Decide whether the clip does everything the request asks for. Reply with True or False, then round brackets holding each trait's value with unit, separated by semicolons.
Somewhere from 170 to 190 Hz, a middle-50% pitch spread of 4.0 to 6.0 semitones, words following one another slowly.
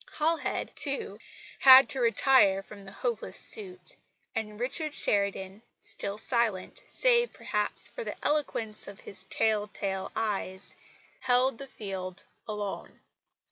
False (220 Hz; 5.2 semitones; 120 wpm)